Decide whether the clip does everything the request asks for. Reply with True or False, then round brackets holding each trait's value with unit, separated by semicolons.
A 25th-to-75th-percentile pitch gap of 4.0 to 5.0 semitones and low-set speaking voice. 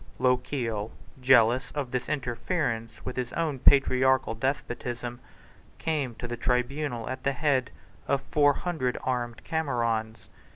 False (2.6 semitones; 125 Hz)